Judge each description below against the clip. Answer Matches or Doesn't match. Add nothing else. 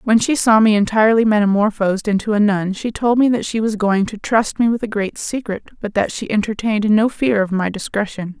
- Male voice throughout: Doesn't match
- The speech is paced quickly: Matches